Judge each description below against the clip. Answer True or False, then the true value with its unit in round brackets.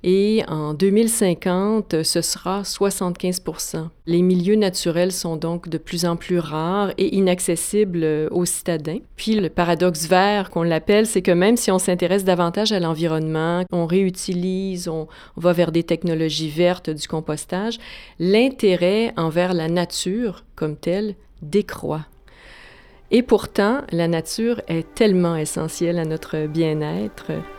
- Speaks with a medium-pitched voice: True (180 Hz)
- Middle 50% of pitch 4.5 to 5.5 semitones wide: False (3.0 semitones)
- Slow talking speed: True (135 wpm)